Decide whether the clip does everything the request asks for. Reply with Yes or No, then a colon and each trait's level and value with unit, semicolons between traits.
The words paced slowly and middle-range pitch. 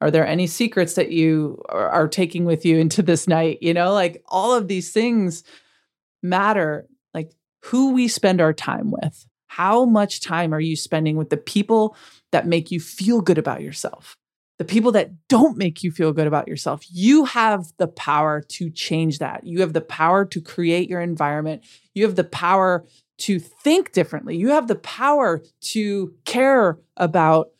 No: average, 180 wpm; medium, 175 Hz